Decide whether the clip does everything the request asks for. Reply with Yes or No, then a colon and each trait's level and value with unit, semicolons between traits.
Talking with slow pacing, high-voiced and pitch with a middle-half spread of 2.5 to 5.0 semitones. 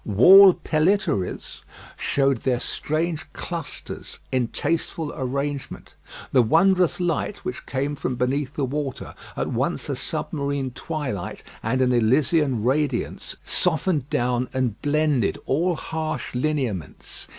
No: slow, 115 wpm; medium, 140 Hz; average, 3.8 semitones